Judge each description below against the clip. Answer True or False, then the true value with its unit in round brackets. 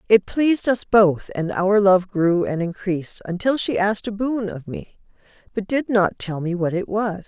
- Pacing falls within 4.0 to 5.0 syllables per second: True (4.7 syllables/s)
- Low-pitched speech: False (200 Hz)